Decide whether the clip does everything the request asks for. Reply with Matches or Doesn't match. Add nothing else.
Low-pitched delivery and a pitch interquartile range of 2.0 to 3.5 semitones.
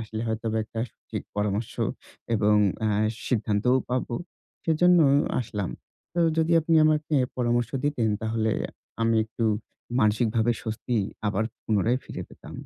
Matches